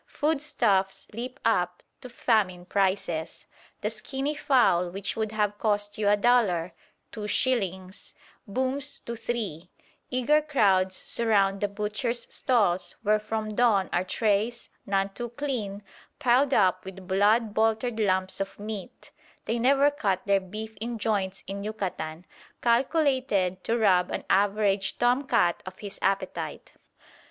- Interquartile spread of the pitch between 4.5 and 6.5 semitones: No, average, 3.7 semitones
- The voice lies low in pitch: No, high, 210 Hz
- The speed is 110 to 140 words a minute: Yes, slow, 135 wpm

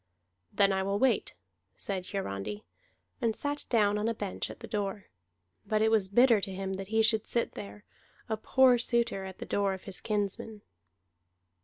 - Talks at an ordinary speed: Yes, average, 180 wpm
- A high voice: Yes, high, 205 Hz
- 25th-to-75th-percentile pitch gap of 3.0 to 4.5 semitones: No, narrow, 2.6 semitones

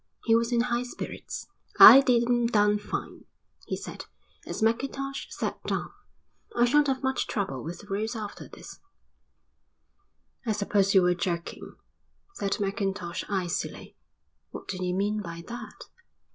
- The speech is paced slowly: No, average, 145 wpm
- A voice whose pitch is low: No, high, 210 Hz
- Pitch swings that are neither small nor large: Yes, average, 3.7 semitones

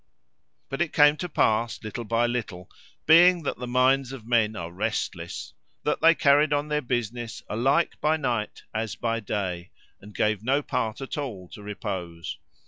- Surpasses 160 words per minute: Yes, average, 170 wpm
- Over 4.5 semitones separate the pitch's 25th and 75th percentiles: Yes, average, 4.9 semitones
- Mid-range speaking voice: No, low, 120 Hz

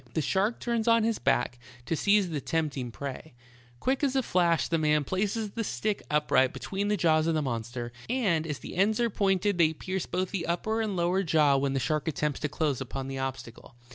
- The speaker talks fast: Yes, fast, 215 wpm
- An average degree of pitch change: No, wide, 6.3 semitones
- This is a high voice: No, medium, 165 Hz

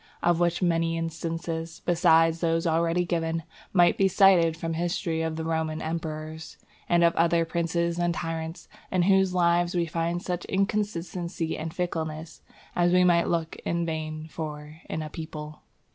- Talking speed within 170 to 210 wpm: No, average, 160 wpm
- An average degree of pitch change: No, narrow, 1.3 semitones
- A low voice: No, medium, 165 Hz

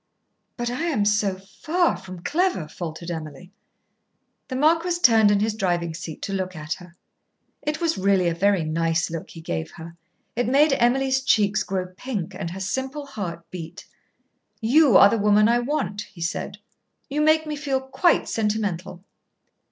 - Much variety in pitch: Yes, wide, 7.1 semitones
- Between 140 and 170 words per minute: Yes, average, 165 wpm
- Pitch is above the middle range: Yes, high, 205 Hz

